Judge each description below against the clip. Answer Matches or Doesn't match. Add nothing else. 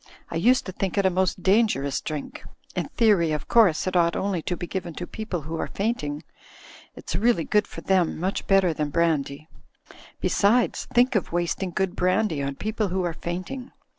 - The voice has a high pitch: Doesn't match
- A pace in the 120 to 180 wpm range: Doesn't match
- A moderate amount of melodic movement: Matches